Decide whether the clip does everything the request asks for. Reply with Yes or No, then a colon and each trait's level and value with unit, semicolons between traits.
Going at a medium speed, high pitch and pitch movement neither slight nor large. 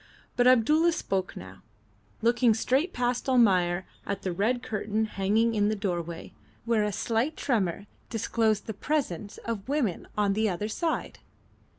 Yes: average, 150 wpm; high, 220 Hz; average, 3.7 semitones